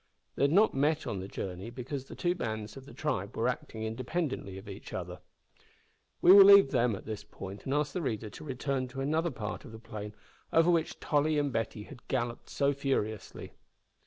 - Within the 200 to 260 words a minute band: Yes, fast, 205 wpm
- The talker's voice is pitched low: Yes, low, 130 Hz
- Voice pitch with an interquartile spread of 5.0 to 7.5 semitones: Yes, wide, 5.5 semitones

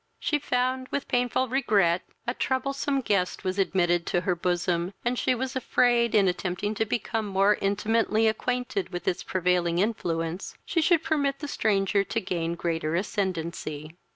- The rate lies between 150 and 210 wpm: Yes, average, 155 wpm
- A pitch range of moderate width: No, wide, 5.9 semitones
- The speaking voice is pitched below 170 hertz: No, high, 200 Hz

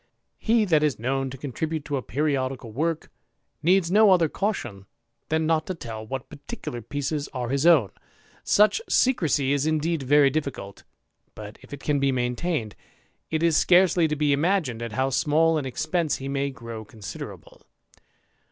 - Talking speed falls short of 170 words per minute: Yes, average, 160 wpm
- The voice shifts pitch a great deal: No, average, 4.0 semitones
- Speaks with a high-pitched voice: No, medium, 145 Hz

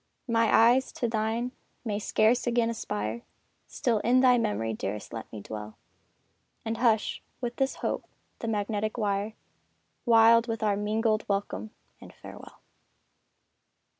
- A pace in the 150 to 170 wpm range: No, slow, 135 wpm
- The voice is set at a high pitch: Yes, high, 220 Hz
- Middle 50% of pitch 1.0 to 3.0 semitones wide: Yes, narrow, 2.4 semitones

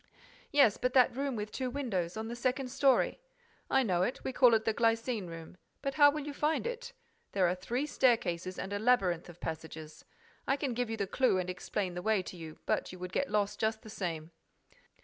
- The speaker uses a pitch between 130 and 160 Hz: No, high, 220 Hz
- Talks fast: Yes, fast, 220 wpm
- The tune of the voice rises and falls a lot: Yes, wide, 6.1 semitones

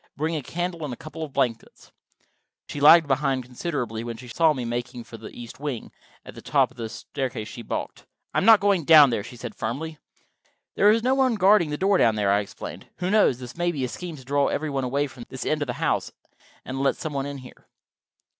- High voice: No, medium, 140 Hz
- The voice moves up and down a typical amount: Yes, average, 5.0 semitones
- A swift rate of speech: Yes, fast, 235 wpm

